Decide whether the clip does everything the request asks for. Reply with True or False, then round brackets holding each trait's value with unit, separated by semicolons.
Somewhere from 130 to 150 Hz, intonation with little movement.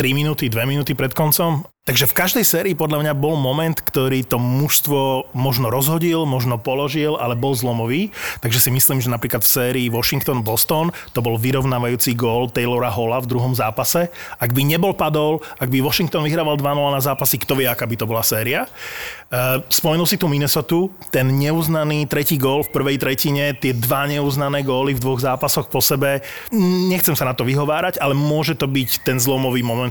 False (140 Hz; 3.1 semitones)